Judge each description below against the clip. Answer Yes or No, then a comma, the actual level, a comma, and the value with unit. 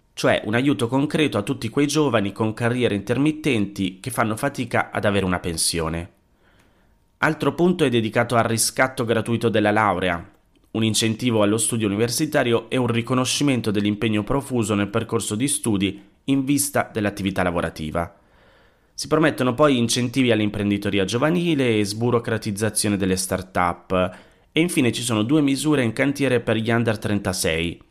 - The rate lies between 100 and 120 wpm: No, average, 145 wpm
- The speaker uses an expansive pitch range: No, average, 4.3 semitones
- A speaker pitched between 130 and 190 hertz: No, low, 115 Hz